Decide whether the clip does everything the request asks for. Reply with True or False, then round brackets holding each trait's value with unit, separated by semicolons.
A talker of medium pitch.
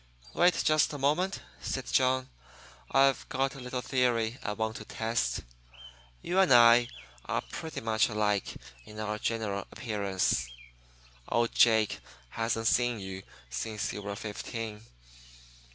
False (115 Hz)